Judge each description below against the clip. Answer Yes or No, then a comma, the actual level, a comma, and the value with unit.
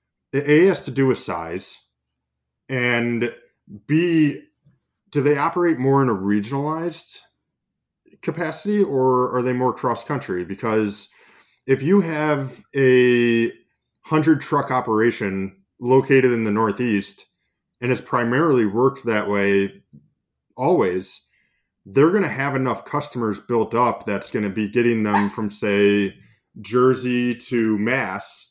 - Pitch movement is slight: No, average, 5.0 semitones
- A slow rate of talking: Yes, slow, 120 wpm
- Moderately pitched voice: No, low, 125 Hz